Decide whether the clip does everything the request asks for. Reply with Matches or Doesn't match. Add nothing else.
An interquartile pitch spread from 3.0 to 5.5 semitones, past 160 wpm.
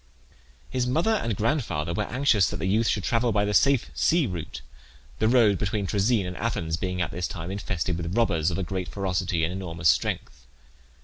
Matches